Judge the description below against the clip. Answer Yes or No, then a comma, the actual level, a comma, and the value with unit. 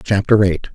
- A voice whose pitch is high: No, low, 100 Hz